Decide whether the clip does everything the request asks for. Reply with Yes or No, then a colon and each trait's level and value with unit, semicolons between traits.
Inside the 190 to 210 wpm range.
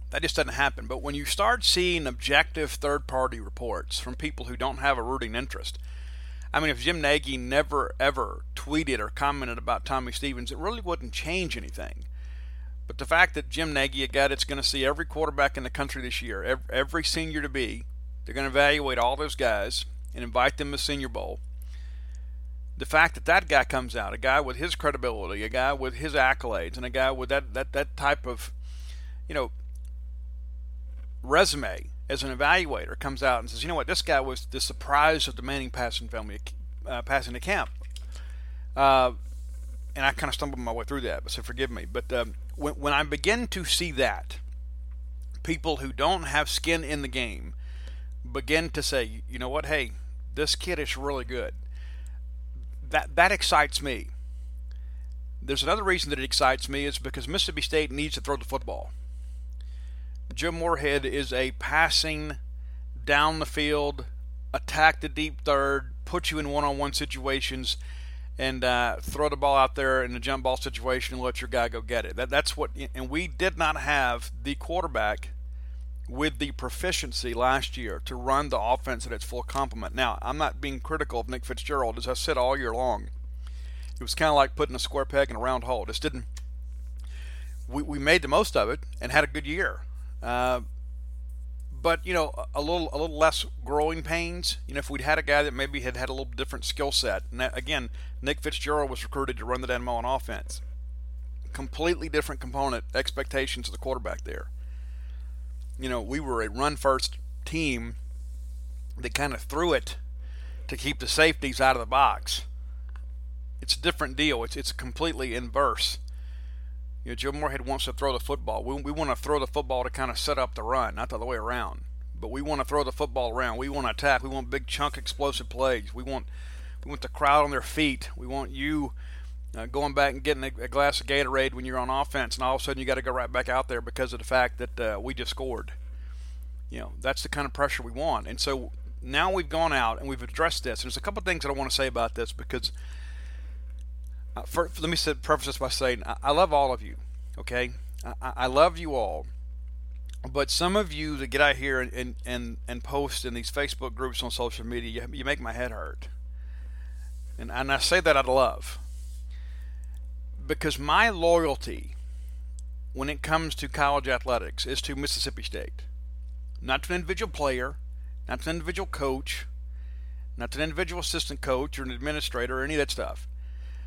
Yes: average, 200 wpm